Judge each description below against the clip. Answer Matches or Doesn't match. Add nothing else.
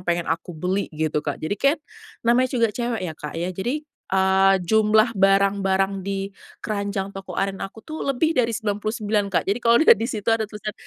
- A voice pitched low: Doesn't match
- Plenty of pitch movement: Doesn't match